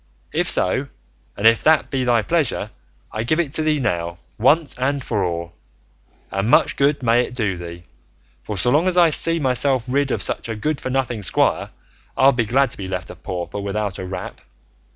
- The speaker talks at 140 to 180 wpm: No, fast, 205 wpm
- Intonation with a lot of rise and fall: Yes, wide, 5.7 semitones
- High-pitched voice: No, low, 120 Hz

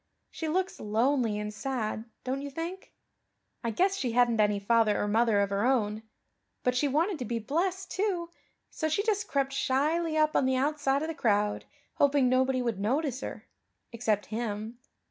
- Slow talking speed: No, average, 180 wpm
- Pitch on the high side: Yes, very high, 260 Hz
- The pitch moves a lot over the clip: Yes, wide, 5.9 semitones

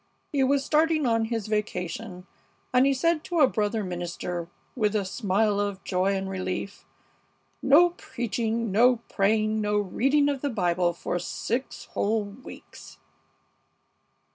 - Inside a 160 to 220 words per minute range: No, average, 140 wpm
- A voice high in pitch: Yes, high, 215 Hz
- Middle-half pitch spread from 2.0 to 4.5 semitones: No, average, 5.0 semitones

